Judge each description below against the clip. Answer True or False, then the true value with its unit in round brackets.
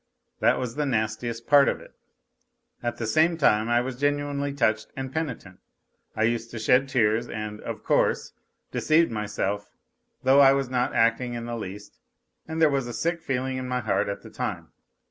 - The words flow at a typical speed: True (185 wpm)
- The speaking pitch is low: True (125 Hz)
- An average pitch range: True (4.0 semitones)